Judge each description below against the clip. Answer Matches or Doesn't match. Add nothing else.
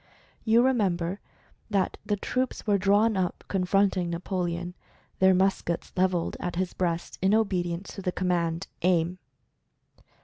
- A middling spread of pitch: Doesn't match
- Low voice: Doesn't match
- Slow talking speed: Matches